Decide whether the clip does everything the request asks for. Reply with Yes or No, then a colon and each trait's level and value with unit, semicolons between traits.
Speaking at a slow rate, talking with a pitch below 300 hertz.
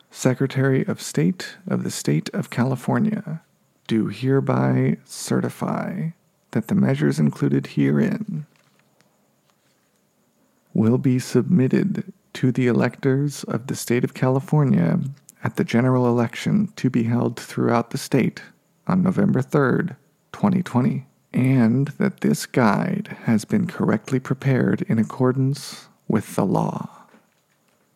Yes: slow, 115 wpm; low, 135 Hz